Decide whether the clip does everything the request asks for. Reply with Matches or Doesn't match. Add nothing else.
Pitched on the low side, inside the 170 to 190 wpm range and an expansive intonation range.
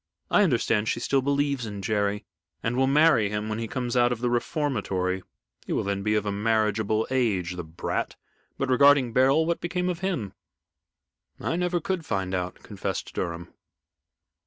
Matches